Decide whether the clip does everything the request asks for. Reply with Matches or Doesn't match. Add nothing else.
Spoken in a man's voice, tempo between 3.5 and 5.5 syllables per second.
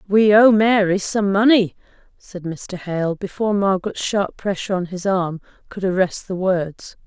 Doesn't match